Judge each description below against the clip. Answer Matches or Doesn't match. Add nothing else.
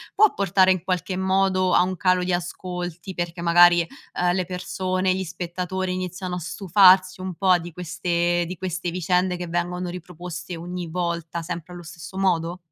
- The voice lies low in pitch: Doesn't match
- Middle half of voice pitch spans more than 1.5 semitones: Doesn't match